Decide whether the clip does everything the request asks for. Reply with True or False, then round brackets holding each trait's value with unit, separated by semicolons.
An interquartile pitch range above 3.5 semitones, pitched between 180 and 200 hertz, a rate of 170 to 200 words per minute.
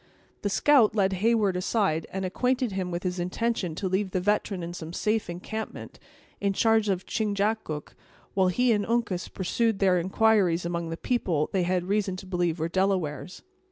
False (3.2 semitones; 190 Hz; 175 wpm)